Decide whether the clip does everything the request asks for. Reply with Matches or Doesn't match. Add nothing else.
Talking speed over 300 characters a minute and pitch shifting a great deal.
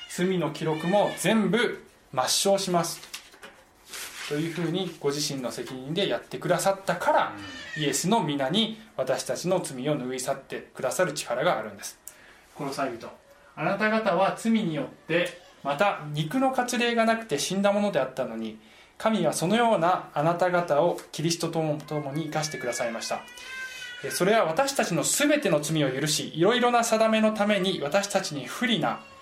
Matches